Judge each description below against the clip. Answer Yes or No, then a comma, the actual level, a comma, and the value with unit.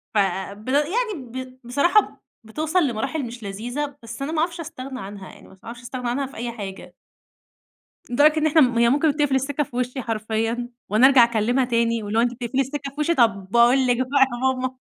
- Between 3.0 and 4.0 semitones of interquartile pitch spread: Yes, average, 3.5 semitones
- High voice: Yes, very high, 250 Hz